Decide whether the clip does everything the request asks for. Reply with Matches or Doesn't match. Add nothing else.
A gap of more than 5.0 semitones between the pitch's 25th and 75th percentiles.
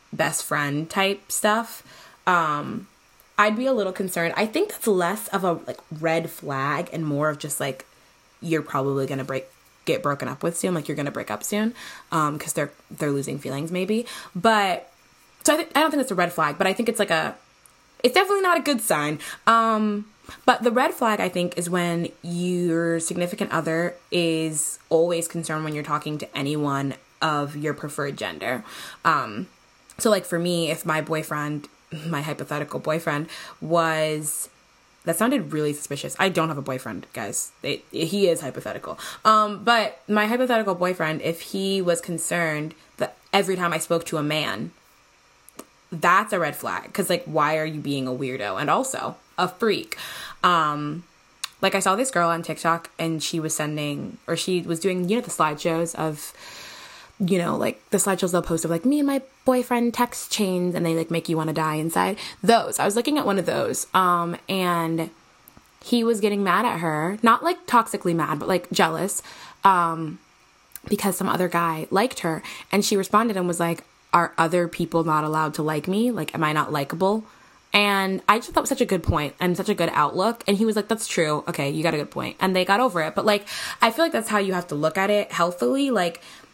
Doesn't match